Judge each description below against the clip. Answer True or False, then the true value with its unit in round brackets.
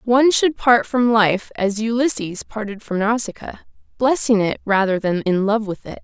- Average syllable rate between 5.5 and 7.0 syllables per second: False (4.7 syllables/s)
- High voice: True (220 Hz)